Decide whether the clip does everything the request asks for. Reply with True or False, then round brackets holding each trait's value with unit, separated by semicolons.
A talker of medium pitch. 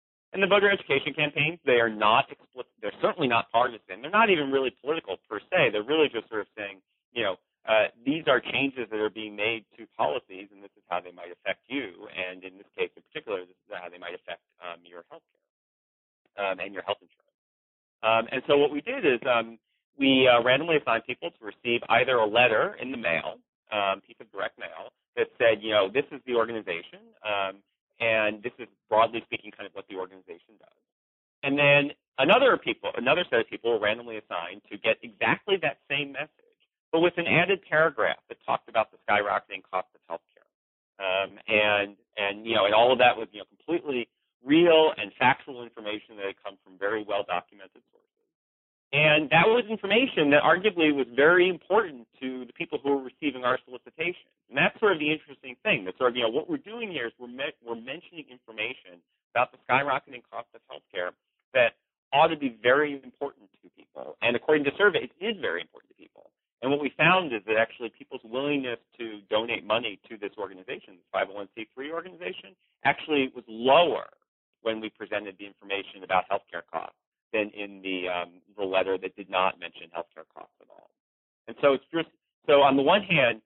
False (125 Hz)